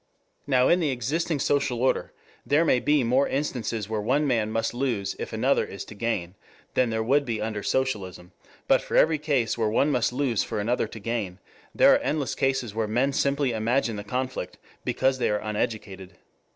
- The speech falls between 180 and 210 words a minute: Yes, average, 190 wpm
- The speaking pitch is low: Yes, low, 120 Hz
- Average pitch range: Yes, average, 4.1 semitones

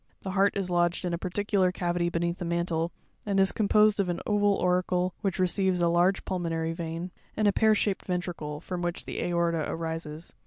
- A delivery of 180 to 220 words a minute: Yes, average, 195 wpm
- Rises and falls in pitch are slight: Yes, narrow, 2.1 semitones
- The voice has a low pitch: No, medium, 180 Hz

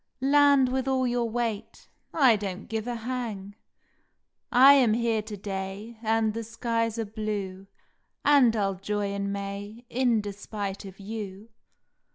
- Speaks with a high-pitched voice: Yes, high, 220 Hz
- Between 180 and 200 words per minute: No, average, 155 wpm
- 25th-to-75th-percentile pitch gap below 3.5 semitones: Yes, average, 3.1 semitones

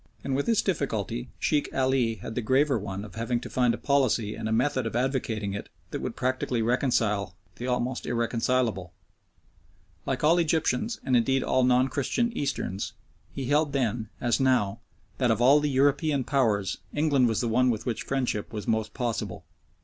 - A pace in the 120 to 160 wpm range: No, average, 180 wpm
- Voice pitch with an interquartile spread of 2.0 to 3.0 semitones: No, average, 3.5 semitones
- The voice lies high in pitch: No, low, 125 Hz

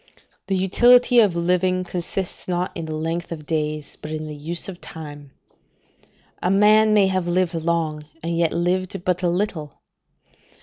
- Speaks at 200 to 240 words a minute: No, average, 165 wpm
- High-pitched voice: No, medium, 175 Hz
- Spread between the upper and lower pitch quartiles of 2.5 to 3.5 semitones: Yes, average, 2.8 semitones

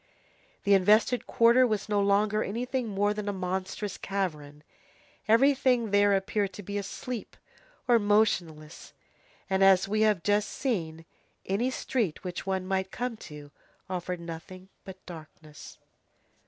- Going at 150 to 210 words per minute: No, slow, 135 wpm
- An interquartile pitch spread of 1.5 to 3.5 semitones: Yes, average, 2.8 semitones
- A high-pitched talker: Yes, high, 200 Hz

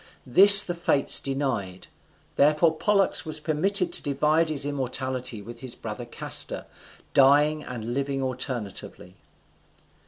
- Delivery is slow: Yes, slow, 120 wpm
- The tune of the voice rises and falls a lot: No, average, 3.6 semitones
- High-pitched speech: No, medium, 140 Hz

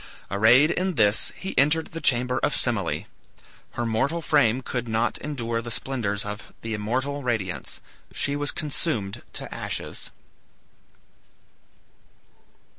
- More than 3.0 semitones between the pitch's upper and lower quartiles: Yes, average, 4.6 semitones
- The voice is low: Yes, low, 120 Hz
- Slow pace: Yes, slow, 120 wpm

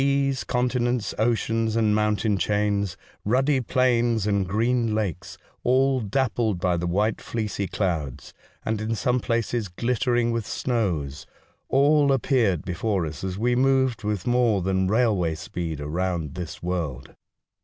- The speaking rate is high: No, average, 145 wpm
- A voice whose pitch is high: No, low, 110 Hz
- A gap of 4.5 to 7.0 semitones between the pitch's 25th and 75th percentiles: Yes, average, 4.8 semitones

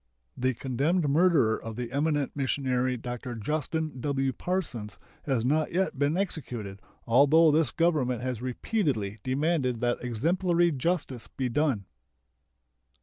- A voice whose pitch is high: No, low, 135 Hz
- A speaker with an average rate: No, slow, 125 wpm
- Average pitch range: Yes, average, 4.4 semitones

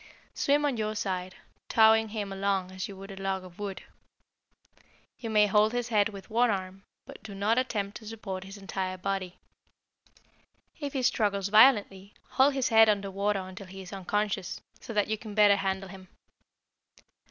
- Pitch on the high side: Yes, high, 200 Hz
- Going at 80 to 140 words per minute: No, average, 175 wpm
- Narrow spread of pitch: Yes, narrow, 2.2 semitones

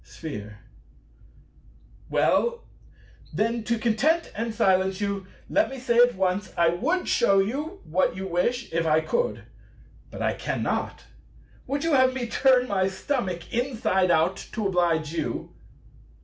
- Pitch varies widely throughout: Yes, wide, 5.8 semitones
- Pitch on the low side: No, high, 210 Hz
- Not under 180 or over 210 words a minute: No, average, 140 wpm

